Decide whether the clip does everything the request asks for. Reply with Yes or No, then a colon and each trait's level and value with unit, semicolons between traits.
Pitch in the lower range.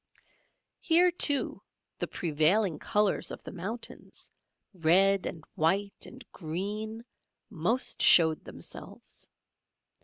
No: high, 195 Hz